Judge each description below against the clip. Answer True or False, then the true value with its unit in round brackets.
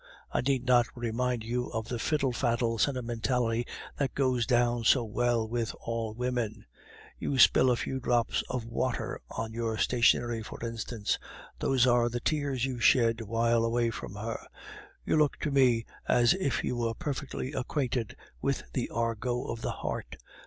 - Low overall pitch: True (120 Hz)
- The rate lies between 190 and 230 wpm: False (165 wpm)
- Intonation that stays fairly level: True (1.8 semitones)